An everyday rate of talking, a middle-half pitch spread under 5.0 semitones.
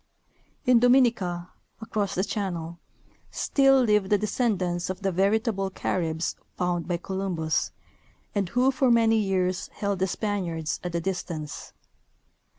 No: slow, 130 wpm; average, 3.9 semitones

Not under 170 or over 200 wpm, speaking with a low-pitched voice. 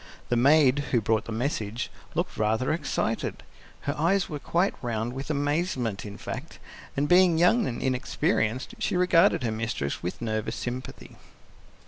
No: average, 150 wpm; low, 130 Hz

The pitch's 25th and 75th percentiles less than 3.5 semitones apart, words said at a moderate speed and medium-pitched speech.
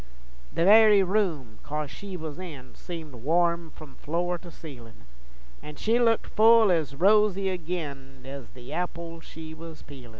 No: average, 4.6 semitones; average, 155 wpm; medium, 165 Hz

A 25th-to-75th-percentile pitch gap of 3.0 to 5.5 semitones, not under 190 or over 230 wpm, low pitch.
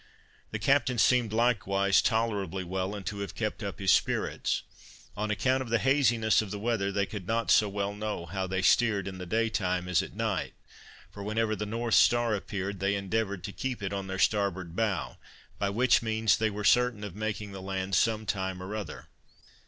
No: narrow, 2.5 semitones; average, 200 wpm; low, 105 Hz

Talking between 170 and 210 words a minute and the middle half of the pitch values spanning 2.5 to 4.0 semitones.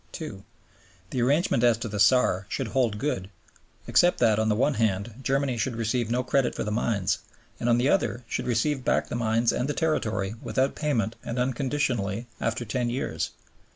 Yes: average, 190 wpm; average, 3.3 semitones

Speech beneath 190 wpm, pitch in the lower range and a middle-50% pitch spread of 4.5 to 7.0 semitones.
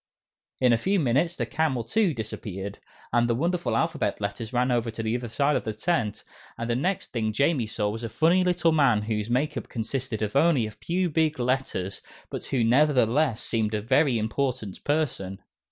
No: average, 195 wpm; low, 125 Hz; wide, 5.5 semitones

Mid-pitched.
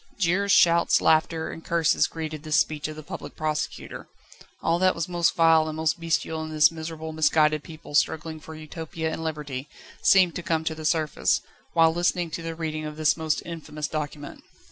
Yes: medium, 160 Hz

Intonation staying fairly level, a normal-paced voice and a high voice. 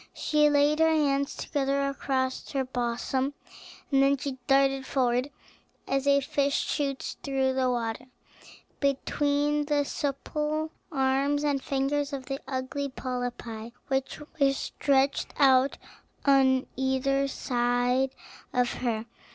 No: narrow, 1.5 semitones; slow, 120 wpm; very high, 275 Hz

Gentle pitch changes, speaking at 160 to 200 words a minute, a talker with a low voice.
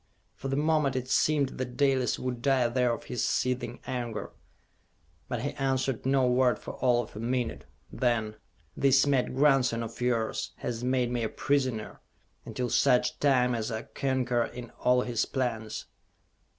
Yes: narrow, 1.9 semitones; average, 165 wpm; low, 125 Hz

